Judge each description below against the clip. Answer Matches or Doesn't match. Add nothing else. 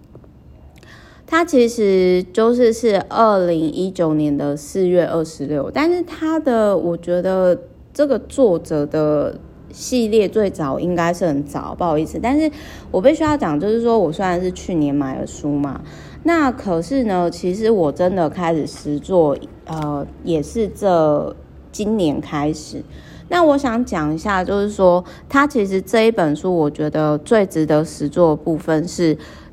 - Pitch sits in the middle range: Matches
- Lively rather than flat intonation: Matches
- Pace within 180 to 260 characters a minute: Matches